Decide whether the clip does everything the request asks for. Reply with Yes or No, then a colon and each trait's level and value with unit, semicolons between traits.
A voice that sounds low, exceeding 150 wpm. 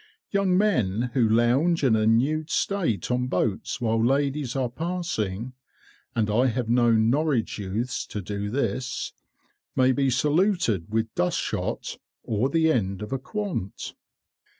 No: low, 125 Hz; average, 145 wpm